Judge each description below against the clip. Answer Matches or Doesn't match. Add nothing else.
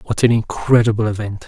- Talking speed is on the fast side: Doesn't match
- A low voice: Matches